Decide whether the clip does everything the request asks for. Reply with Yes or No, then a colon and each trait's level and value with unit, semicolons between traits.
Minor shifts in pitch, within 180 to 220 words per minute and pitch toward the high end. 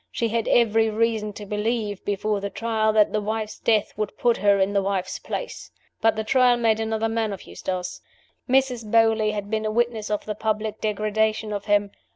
Yes: narrow, 1.4 semitones; average, 200 wpm; high, 215 Hz